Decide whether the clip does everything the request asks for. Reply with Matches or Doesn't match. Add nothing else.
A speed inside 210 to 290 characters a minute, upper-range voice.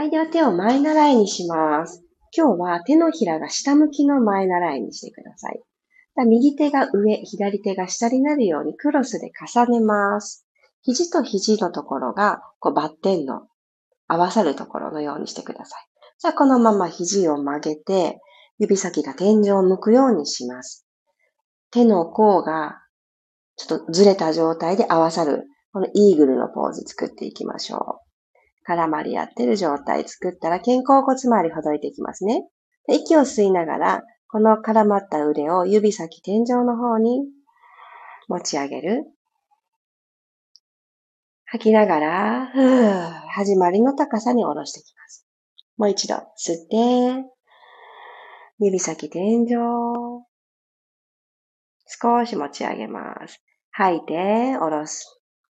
Matches